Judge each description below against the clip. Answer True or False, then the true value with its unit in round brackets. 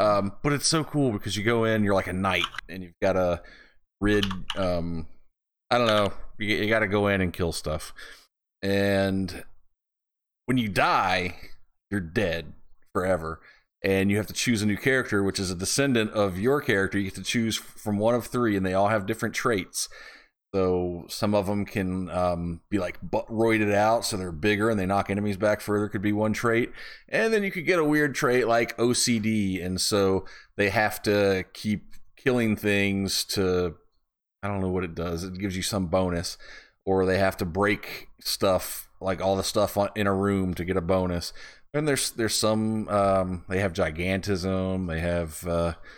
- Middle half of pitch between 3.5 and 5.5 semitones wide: False (2.7 semitones)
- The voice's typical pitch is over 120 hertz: False (100 Hz)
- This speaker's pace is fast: False (190 wpm)